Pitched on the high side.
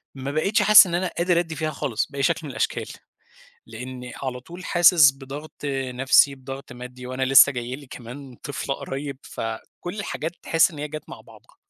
No: medium, 140 Hz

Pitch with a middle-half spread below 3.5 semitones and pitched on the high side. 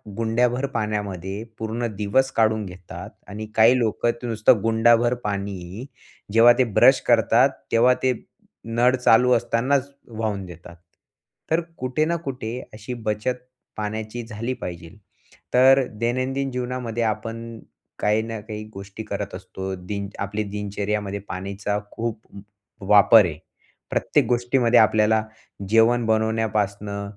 No: average, 2.8 semitones; low, 110 Hz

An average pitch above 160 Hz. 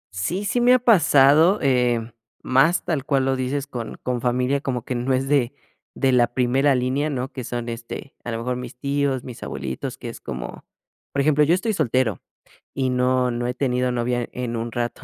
No: low, 130 Hz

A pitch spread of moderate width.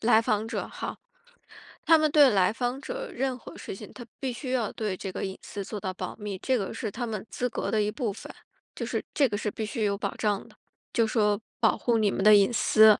Yes: average, 3.3 semitones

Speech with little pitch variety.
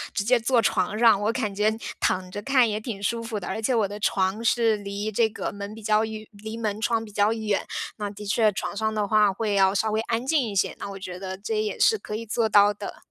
Yes: narrow, 1.8 semitones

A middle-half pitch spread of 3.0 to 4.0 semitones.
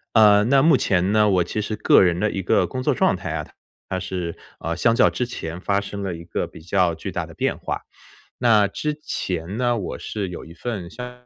No: average, 4.5 semitones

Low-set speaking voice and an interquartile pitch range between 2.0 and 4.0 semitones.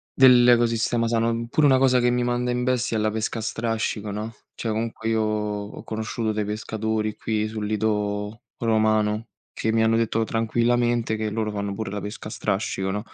No: low, 110 Hz; narrow, 1.5 semitones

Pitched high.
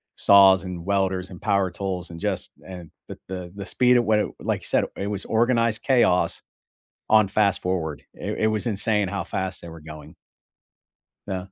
No: very low, 95 Hz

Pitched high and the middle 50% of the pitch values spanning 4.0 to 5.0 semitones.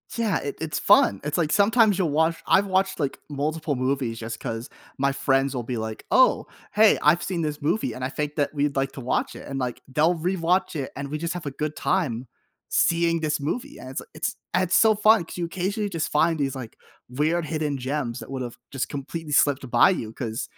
No: medium, 150 Hz; average, 4.3 semitones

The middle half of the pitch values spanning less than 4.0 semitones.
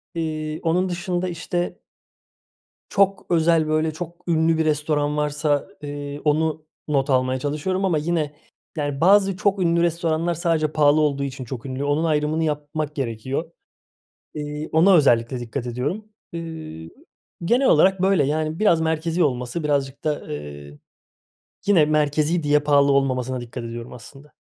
Yes: average, 2.8 semitones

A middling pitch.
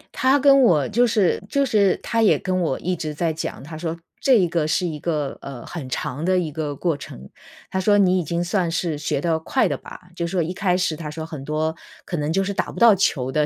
Yes: medium, 170 Hz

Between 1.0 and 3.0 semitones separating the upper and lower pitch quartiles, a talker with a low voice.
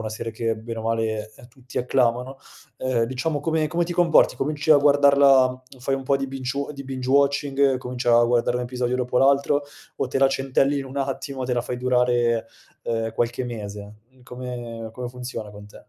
Yes: narrow, 2.5 semitones; low, 125 Hz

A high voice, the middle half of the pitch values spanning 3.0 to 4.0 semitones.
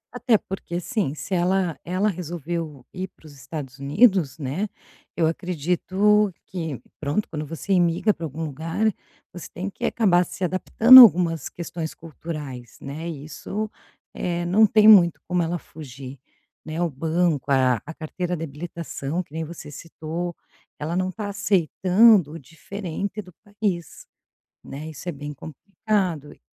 No: medium, 170 Hz; average, 3.6 semitones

